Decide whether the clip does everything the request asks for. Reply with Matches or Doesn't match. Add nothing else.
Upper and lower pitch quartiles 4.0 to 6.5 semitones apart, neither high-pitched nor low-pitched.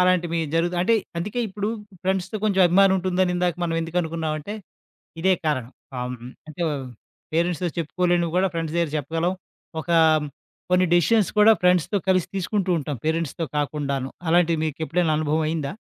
Doesn't match